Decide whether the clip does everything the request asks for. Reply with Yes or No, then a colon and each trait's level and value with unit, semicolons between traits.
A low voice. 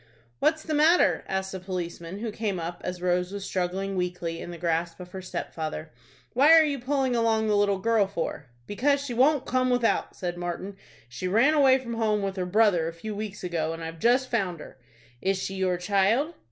No: high, 195 Hz